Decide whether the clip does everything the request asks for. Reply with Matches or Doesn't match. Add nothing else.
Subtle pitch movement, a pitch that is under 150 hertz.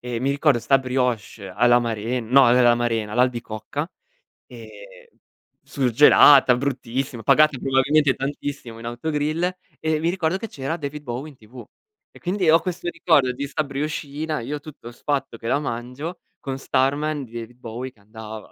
Doesn't match